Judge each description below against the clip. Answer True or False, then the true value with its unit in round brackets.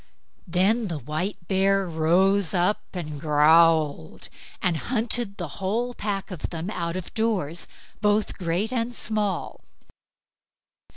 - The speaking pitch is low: False (185 Hz)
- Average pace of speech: False (120 wpm)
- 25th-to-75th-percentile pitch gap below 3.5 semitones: False (4.1 semitones)